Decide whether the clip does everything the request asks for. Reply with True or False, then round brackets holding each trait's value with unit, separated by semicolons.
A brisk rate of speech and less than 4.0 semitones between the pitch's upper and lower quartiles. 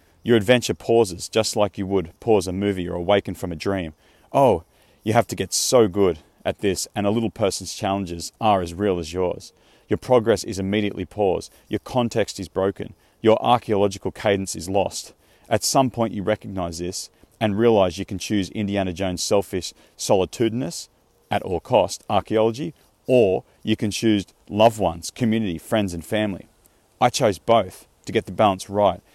False (175 wpm; 3.0 semitones)